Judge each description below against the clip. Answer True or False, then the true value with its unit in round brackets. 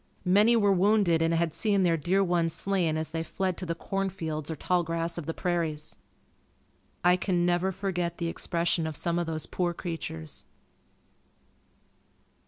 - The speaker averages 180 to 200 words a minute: False (170 wpm)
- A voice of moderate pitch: True (175 Hz)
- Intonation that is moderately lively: False (2.3 semitones)